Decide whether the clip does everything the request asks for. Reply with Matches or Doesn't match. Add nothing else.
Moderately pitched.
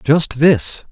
Matches